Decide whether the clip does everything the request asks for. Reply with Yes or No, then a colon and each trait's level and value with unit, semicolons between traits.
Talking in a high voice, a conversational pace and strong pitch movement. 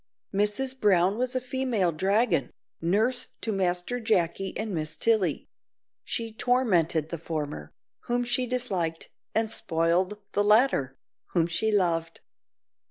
No: high, 200 Hz; slow, 125 wpm; wide, 6.1 semitones